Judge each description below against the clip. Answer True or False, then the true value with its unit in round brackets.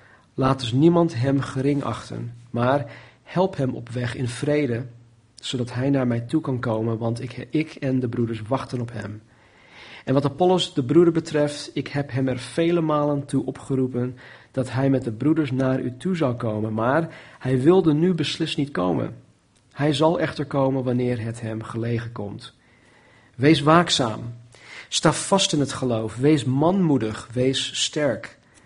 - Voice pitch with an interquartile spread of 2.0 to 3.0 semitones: False (3.8 semitones)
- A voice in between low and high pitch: False (130 Hz)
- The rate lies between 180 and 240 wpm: False (170 wpm)